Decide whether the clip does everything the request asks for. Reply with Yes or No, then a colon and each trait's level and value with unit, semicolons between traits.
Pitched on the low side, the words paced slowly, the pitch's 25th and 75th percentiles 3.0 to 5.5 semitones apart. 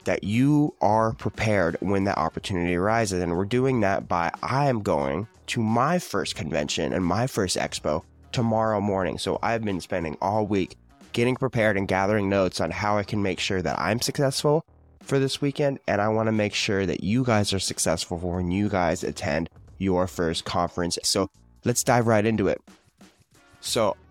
No: low, 100 Hz; average, 185 wpm; average, 4.3 semitones